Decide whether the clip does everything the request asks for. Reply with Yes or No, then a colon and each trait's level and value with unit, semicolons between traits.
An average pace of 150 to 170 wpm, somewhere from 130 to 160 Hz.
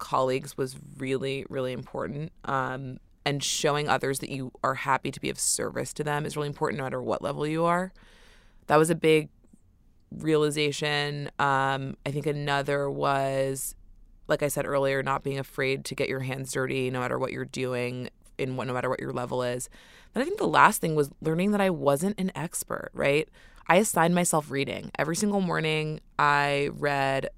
No: average, 190 wpm; medium, 140 Hz